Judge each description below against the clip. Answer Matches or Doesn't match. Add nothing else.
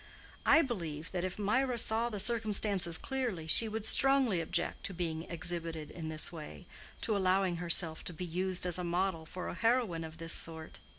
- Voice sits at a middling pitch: Matches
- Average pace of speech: Matches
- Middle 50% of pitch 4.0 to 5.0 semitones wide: Matches